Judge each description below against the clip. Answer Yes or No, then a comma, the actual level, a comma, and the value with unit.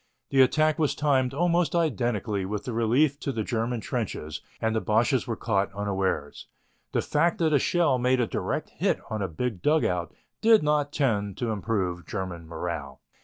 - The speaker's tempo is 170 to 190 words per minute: Yes, average, 175 wpm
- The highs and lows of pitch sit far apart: Yes, wide, 6.4 semitones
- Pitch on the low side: Yes, low, 120 Hz